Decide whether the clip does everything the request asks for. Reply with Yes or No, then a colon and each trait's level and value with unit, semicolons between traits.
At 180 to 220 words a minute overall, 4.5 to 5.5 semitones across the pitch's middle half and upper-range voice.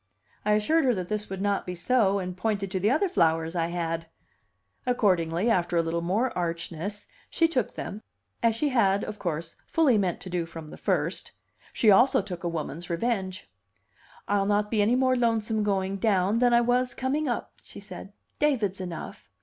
Yes: average, 190 wpm; average, 5.2 semitones; high, 200 Hz